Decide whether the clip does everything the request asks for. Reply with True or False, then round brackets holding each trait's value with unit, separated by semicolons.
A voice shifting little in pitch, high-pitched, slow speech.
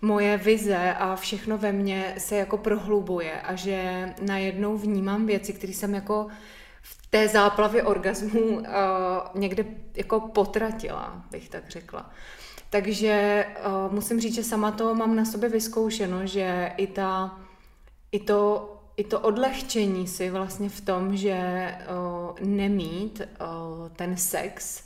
False (2.1 semitones; 200 Hz; 140 wpm)